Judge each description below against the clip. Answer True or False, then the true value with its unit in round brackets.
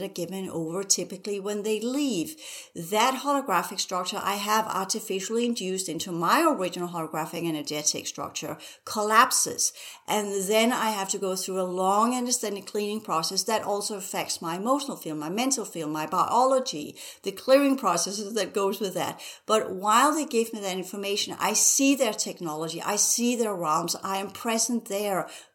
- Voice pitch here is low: False (200 Hz)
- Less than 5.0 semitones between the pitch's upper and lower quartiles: True (3.4 semitones)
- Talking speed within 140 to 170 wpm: True (165 wpm)